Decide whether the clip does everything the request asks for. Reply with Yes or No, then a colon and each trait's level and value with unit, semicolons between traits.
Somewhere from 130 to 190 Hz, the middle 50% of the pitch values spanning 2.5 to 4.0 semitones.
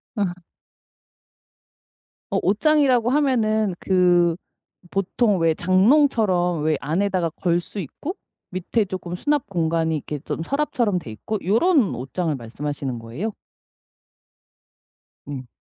No: medium, 185 Hz; wide, 5.6 semitones